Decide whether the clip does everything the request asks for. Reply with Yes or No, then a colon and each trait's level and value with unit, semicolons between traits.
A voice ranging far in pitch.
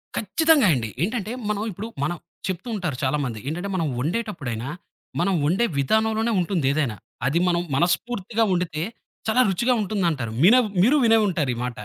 Yes: wide, 6.7 semitones